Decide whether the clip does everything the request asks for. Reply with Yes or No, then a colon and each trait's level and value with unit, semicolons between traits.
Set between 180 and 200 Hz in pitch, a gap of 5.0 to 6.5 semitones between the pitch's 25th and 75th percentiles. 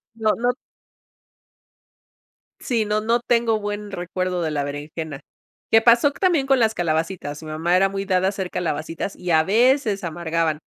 Yes: high, 190 Hz; wide, 5.4 semitones